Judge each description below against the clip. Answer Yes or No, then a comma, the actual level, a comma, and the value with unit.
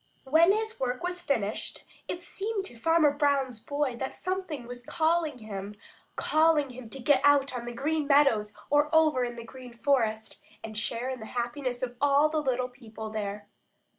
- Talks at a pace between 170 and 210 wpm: Yes, average, 180 wpm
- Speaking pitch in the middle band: No, very high, 265 Hz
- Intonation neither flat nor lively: Yes, average, 4.3 semitones